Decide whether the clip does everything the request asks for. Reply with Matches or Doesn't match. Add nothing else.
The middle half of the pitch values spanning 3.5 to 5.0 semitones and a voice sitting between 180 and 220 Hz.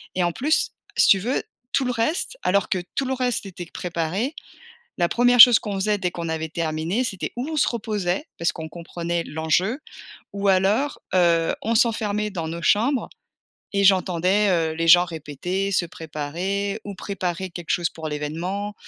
Matches